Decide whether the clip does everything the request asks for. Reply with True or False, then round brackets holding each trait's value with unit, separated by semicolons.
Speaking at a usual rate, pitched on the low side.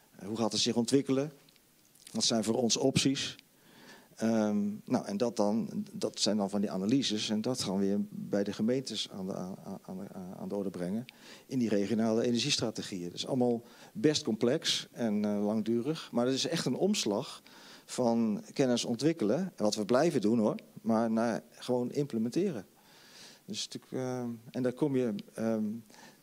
True (170 wpm; 120 Hz)